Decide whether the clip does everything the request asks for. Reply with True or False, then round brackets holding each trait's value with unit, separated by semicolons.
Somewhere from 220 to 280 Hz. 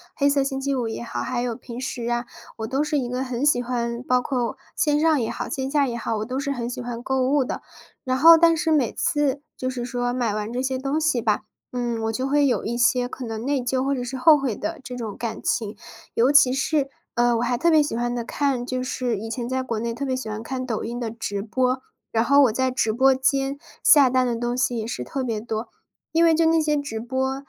True (255 Hz)